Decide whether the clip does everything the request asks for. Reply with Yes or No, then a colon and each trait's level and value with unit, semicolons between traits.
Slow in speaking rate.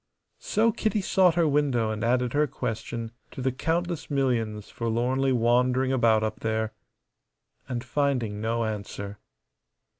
Yes: slow, 130 wpm